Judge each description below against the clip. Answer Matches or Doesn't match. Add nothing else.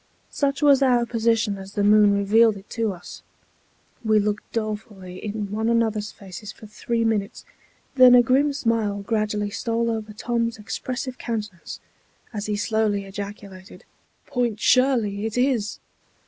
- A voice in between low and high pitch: Doesn't match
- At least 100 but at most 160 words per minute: Matches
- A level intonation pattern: Matches